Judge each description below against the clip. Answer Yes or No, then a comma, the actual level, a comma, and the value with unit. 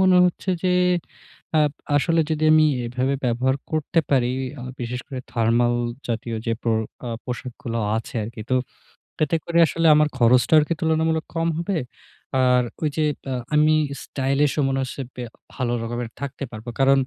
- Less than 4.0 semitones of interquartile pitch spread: No, average, 4.4 semitones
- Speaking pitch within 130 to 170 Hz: Yes, low, 135 Hz